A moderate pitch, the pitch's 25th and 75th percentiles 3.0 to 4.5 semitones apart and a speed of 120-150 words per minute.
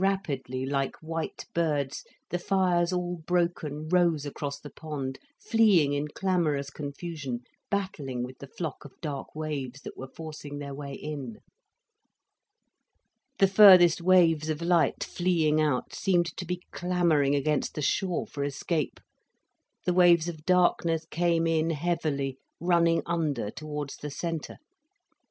Yes: medium, 160 Hz; average, 3.5 semitones; slow, 135 wpm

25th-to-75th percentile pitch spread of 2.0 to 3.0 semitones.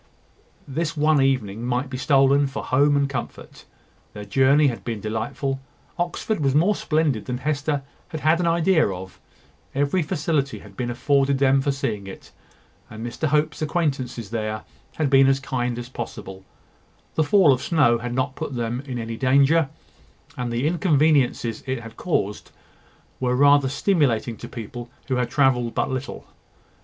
No: average, 3.6 semitones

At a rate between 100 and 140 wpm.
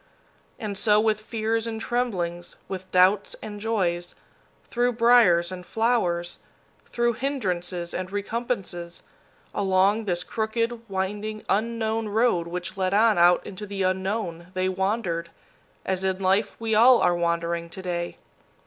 Yes: slow, 135 wpm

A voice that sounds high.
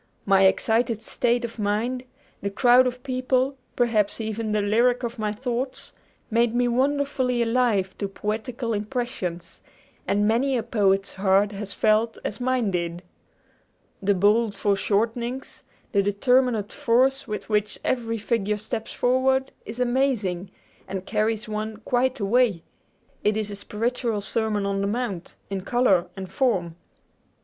Yes: high, 225 Hz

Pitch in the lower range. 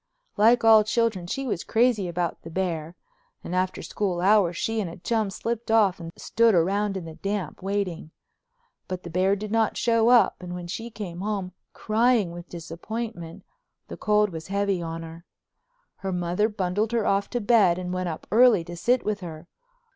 No: high, 195 Hz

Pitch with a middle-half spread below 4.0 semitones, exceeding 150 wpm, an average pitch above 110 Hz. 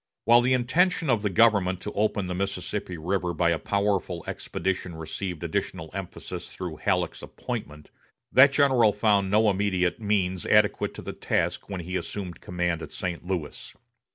No: average, 3.0 semitones; average, 160 wpm; very low, 95 Hz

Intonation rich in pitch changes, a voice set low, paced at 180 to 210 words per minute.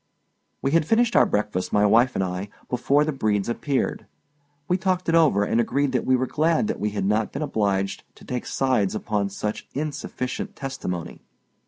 Yes: wide, 6.1 semitones; low, 125 Hz; average, 185 wpm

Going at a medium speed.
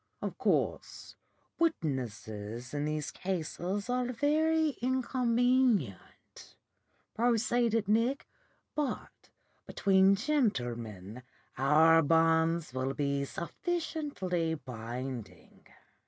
No: slow, 75 wpm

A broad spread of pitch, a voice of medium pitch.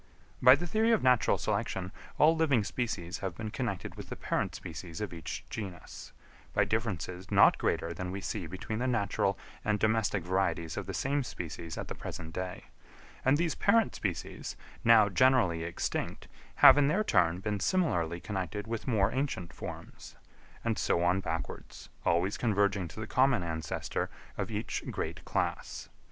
No: wide, 6.1 semitones; low, 100 Hz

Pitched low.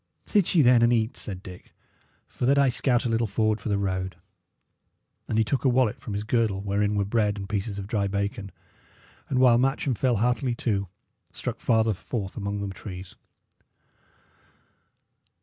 Yes: low, 110 Hz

